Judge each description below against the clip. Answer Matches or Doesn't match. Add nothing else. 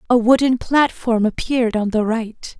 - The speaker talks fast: Doesn't match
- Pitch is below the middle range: Doesn't match